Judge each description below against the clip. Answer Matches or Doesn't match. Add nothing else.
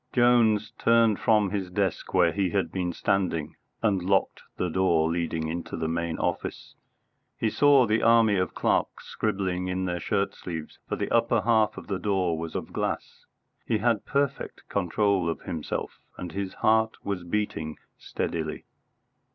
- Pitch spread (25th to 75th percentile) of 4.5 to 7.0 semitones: Doesn't match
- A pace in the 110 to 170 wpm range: Matches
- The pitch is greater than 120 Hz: Doesn't match